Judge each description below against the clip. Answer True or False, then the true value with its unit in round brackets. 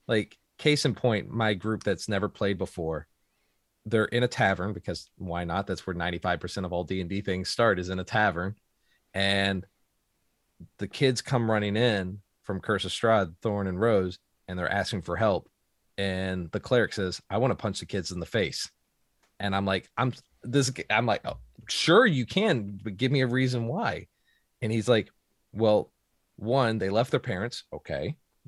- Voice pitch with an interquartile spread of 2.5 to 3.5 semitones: True (3.2 semitones)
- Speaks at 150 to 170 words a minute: False (190 wpm)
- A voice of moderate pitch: False (100 Hz)